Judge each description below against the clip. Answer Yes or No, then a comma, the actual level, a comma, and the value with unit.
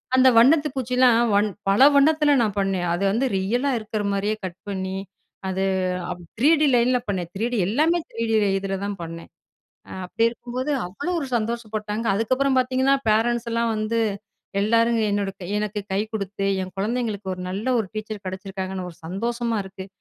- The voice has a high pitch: Yes, high, 215 Hz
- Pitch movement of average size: Yes, average, 3.7 semitones